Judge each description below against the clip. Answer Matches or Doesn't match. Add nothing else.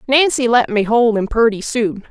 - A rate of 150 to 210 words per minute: Matches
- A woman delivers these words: Matches